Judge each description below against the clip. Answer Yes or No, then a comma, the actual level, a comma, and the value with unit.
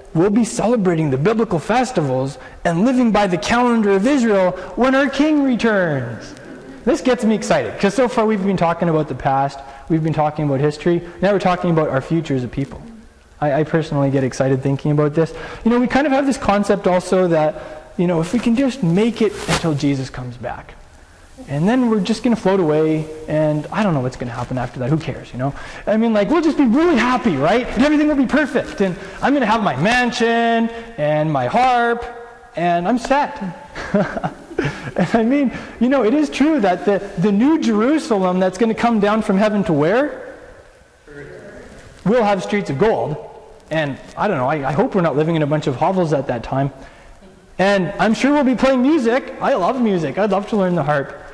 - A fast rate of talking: Yes, fast, 210 wpm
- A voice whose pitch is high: Yes, high, 195 Hz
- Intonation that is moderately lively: No, wide, 7.4 semitones